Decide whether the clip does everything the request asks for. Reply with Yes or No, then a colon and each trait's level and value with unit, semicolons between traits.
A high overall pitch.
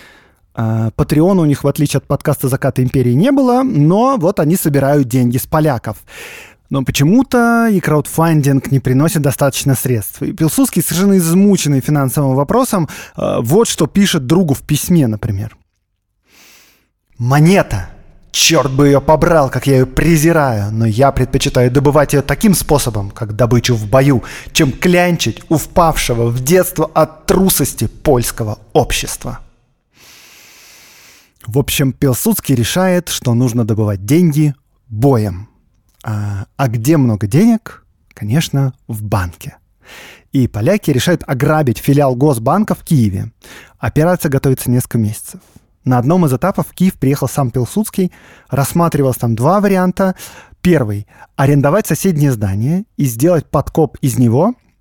No: medium, 140 Hz